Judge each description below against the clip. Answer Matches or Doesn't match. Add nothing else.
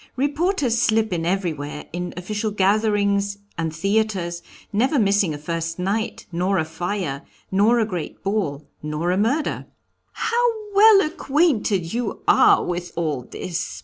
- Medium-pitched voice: Doesn't match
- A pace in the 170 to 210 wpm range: Doesn't match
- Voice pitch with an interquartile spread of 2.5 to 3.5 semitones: Doesn't match